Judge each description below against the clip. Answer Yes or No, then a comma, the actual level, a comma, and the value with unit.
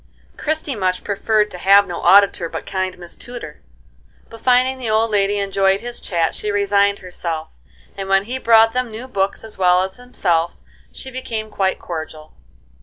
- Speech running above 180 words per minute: No, average, 175 wpm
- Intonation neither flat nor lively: Yes, average, 3.5 semitones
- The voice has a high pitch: Yes, high, 200 Hz